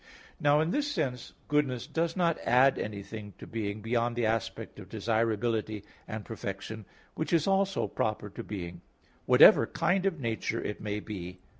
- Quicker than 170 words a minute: No, average, 160 wpm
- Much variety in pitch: Yes, wide, 5.8 semitones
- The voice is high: No, low, 115 Hz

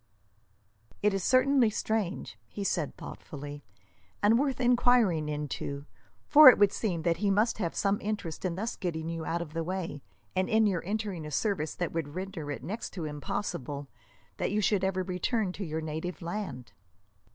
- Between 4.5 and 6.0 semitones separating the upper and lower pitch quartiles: Yes, average, 4.8 semitones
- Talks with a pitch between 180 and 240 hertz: Yes, medium, 185 Hz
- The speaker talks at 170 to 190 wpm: Yes, average, 175 wpm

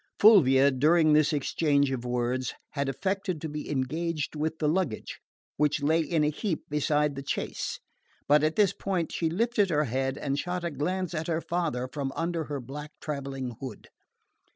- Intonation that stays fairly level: No, average, 3.5 semitones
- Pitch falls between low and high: Yes, medium, 150 Hz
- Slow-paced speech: No, average, 175 wpm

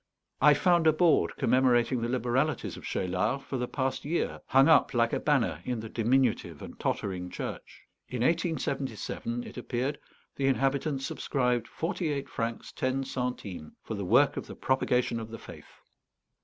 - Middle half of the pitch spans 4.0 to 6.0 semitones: No, average, 3.1 semitones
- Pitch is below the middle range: Yes, low, 130 Hz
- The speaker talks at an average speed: Yes, average, 165 wpm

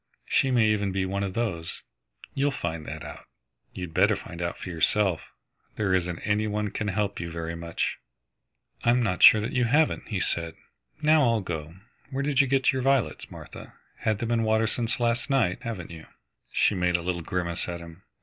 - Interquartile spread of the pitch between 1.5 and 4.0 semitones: No, average, 5.2 semitones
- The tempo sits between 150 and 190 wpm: No, average, 200 wpm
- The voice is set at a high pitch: No, low, 100 Hz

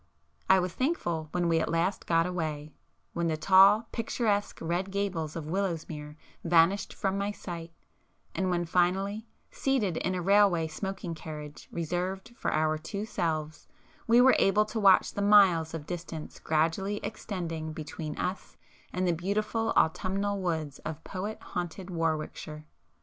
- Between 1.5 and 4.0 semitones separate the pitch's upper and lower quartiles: Yes, average, 3.6 semitones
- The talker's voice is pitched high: No, medium, 180 Hz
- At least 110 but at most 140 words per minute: No, average, 150 wpm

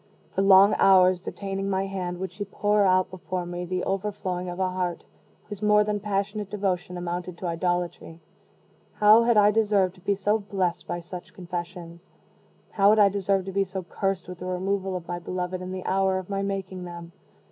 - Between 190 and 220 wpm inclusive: Yes, average, 195 wpm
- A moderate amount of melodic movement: No, narrow, 1.8 semitones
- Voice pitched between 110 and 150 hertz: No, high, 190 Hz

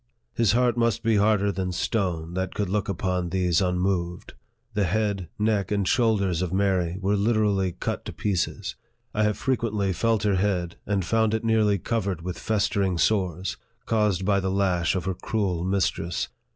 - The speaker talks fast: No, average, 170 wpm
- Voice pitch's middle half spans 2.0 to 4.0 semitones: Yes, average, 2.7 semitones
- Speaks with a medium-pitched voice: No, low, 100 Hz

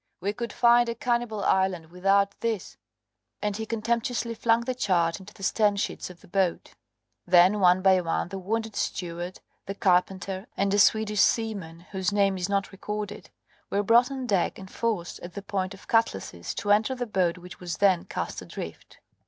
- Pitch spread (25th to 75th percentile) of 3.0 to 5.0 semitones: Yes, average, 3.3 semitones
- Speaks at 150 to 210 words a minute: Yes, average, 185 wpm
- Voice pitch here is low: No, high, 200 Hz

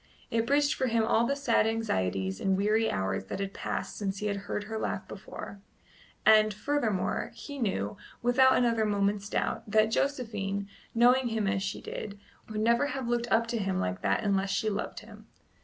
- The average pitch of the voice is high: Yes, high, 215 Hz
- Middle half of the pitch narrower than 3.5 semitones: Yes, average, 3.0 semitones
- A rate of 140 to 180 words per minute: No, average, 190 wpm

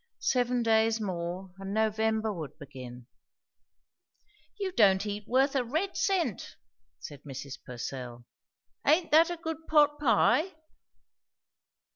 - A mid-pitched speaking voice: No, high, 220 Hz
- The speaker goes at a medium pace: No, slow, 115 wpm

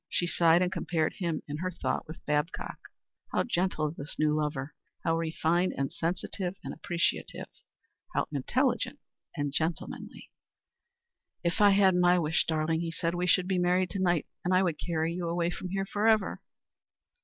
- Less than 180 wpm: Yes, average, 165 wpm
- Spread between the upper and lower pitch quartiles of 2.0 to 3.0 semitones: Yes, narrow, 2.4 semitones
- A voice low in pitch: No, medium, 170 Hz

